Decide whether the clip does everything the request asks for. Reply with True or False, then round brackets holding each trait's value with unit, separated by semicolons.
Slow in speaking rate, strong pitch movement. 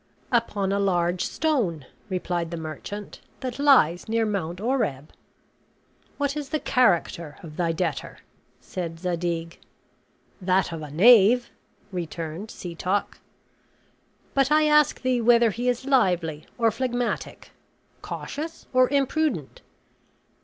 True (115 wpm; 6.8 semitones)